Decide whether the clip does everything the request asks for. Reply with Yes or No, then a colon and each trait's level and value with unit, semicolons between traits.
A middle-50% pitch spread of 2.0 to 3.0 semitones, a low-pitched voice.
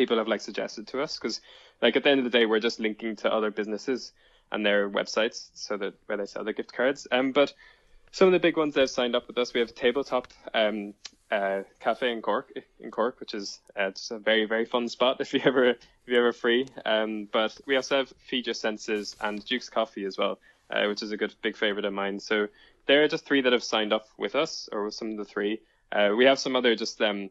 No: average, 3.7 semitones; low, 115 Hz